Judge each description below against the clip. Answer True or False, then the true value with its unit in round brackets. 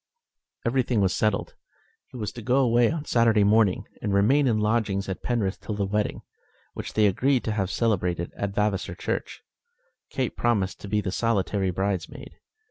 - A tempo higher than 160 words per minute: True (170 wpm)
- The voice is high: False (105 Hz)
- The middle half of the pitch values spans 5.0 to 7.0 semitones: False (3.2 semitones)